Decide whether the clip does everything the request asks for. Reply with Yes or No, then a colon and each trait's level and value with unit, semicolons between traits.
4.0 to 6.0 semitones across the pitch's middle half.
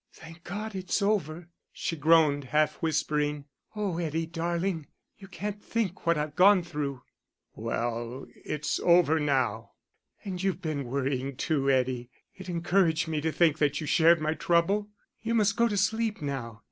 Yes: average, 4.6 semitones